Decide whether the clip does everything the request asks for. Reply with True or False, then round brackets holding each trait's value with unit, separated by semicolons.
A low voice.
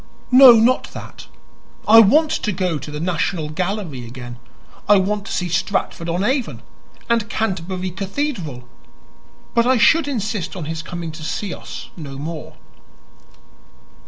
False (185 Hz)